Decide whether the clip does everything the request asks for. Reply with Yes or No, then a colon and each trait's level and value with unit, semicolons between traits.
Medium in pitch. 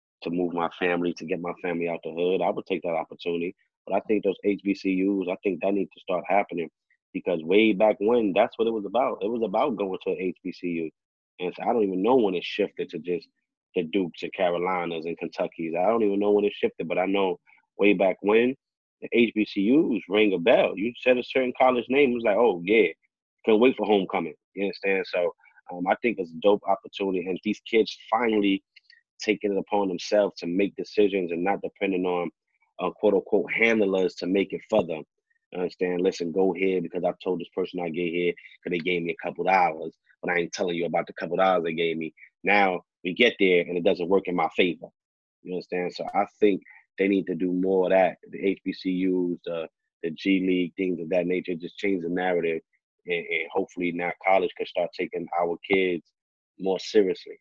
No: very low, 95 Hz